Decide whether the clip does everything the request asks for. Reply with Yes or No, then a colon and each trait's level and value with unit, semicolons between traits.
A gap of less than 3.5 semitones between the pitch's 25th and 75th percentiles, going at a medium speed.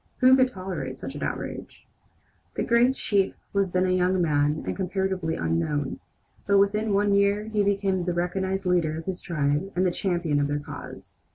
No: average, 4.2 semitones; average, 185 wpm